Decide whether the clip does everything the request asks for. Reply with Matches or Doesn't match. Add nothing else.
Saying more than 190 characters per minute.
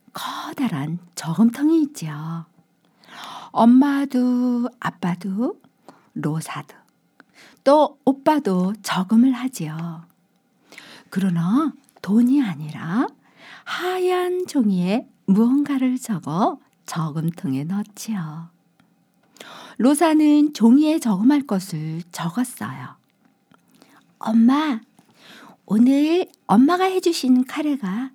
Doesn't match